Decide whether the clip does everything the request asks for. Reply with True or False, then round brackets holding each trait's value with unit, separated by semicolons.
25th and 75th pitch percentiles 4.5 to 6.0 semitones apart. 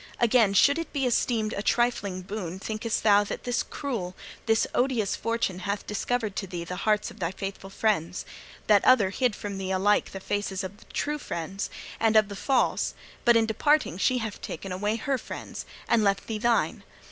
False (3.5 semitones)